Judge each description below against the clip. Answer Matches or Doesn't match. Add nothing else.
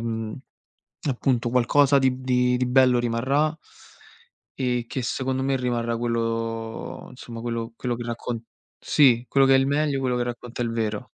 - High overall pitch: Doesn't match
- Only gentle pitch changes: Matches